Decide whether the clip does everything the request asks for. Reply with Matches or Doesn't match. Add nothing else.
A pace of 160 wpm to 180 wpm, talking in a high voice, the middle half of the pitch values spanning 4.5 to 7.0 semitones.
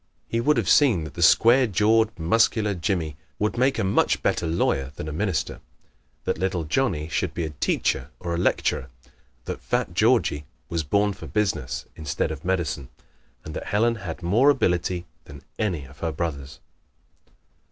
Doesn't match